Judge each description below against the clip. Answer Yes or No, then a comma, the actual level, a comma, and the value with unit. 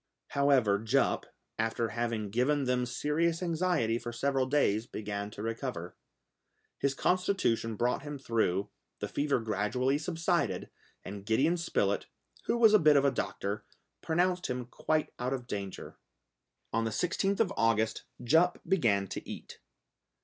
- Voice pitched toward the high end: No, low, 125 Hz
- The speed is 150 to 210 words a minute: No, average, 140 wpm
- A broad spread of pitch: Yes, wide, 5.7 semitones